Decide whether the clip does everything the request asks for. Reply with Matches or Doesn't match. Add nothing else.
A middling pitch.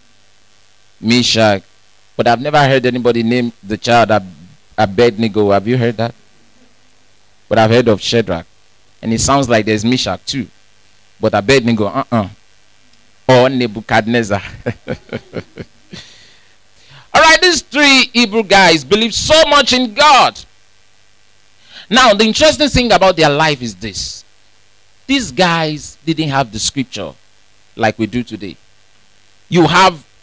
Doesn't match